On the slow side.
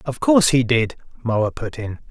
No: average, 200 wpm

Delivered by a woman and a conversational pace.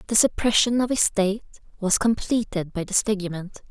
Yes: female; average, 145 wpm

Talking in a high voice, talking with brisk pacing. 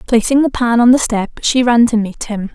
Yes: high, 235 Hz; fast, 260 wpm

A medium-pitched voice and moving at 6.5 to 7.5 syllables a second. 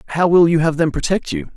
Yes: medium, 155 Hz; 6.6 syllables/s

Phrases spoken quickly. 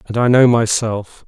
No: average, 190 wpm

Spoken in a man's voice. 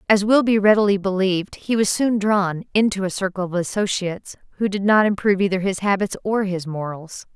No: female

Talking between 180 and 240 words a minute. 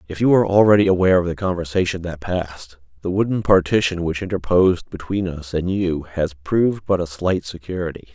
Yes: average, 185 wpm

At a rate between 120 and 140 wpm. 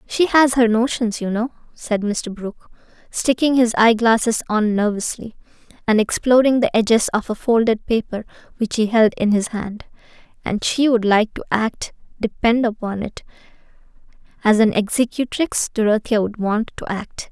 No: average, 155 wpm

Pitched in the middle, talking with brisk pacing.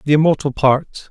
No: medium, 145 Hz; average, 160 wpm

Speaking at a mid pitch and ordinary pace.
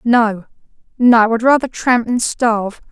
No: high, 230 Hz; average, 145 wpm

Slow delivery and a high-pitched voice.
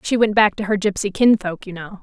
No: fast, 265 wpm; high, 200 Hz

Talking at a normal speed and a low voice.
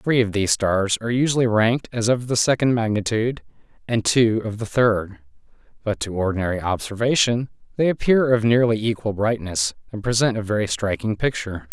Yes: average, 170 wpm; low, 110 Hz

